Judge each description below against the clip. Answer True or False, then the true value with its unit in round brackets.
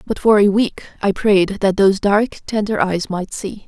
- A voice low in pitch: False (200 Hz)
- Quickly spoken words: True (215 wpm)